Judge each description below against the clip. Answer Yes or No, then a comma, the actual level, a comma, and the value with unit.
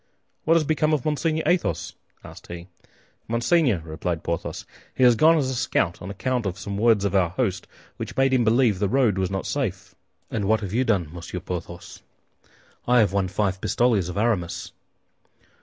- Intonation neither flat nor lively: No, wide, 5.9 semitones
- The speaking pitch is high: No, low, 105 Hz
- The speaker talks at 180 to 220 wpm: Yes, average, 190 wpm